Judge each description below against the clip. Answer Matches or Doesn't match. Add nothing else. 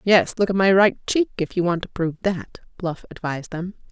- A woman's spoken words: Matches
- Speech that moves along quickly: Matches